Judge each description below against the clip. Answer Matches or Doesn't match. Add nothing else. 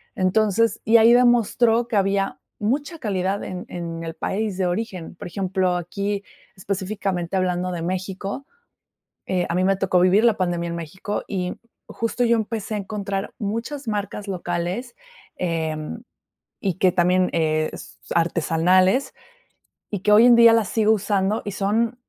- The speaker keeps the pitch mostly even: Doesn't match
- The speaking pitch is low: Doesn't match